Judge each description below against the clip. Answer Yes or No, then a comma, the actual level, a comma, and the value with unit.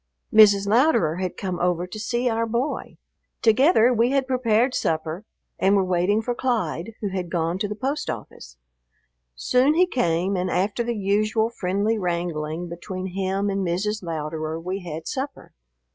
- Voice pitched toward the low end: No, high, 195 Hz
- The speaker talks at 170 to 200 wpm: No, average, 160 wpm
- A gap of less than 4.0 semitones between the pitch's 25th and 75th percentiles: No, average, 4.7 semitones